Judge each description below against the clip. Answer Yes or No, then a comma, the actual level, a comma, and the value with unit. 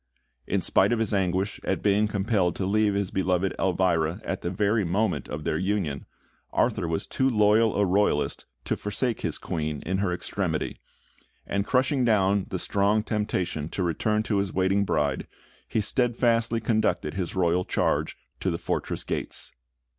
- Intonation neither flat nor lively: Yes, average, 3.1 semitones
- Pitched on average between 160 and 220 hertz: No, low, 100 Hz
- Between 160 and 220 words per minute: Yes, average, 165 wpm